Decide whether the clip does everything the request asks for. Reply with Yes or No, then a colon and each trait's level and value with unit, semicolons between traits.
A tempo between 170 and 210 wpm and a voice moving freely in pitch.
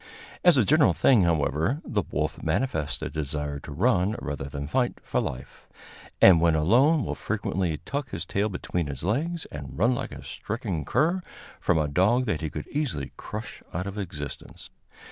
Yes: average, 180 wpm; wide, 8.4 semitones